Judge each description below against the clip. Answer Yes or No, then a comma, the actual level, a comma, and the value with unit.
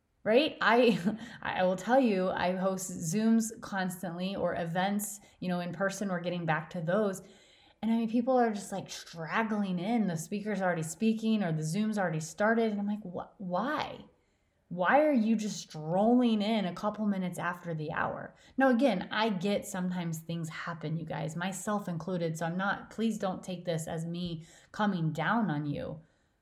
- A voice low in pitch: No, high, 190 Hz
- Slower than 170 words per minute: No, average, 180 wpm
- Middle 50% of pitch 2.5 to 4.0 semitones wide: Yes, average, 3.6 semitones